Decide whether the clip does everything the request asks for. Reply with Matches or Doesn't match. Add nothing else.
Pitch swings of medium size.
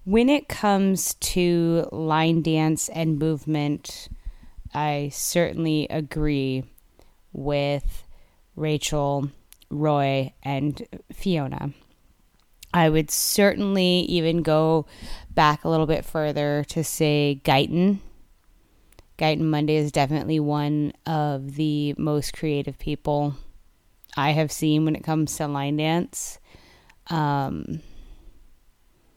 Doesn't match